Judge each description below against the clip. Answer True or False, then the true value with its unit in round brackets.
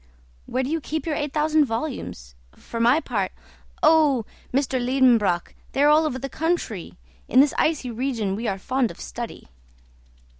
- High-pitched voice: True (260 Hz)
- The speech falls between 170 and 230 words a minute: True (175 wpm)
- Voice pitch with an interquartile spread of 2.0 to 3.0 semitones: False (4.8 semitones)